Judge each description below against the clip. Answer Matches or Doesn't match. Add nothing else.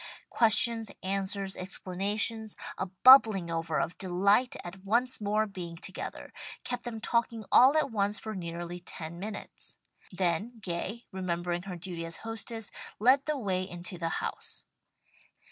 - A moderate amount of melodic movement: Matches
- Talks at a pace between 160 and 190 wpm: Doesn't match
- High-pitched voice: Matches